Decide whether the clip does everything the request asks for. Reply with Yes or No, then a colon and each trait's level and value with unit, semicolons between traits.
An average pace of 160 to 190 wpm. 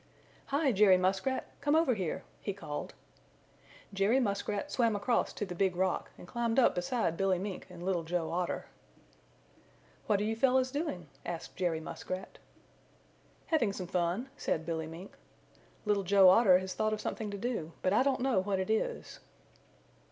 Yes: average, 165 wpm